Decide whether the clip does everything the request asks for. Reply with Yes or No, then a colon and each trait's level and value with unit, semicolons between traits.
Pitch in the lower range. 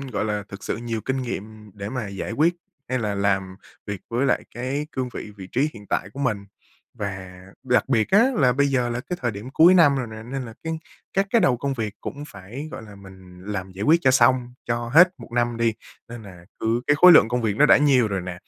Yes: low, 120 Hz